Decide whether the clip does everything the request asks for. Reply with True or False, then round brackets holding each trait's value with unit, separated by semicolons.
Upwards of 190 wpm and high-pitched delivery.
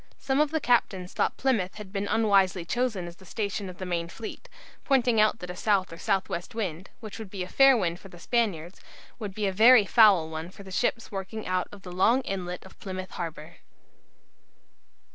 True (205 wpm; 195 Hz)